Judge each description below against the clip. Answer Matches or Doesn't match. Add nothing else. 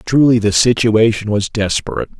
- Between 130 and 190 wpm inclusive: Matches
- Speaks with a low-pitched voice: Matches